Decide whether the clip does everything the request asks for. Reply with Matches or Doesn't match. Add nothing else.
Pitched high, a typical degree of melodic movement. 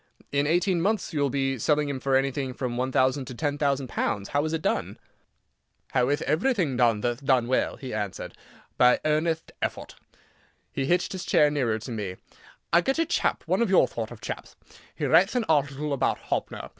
Doesn't match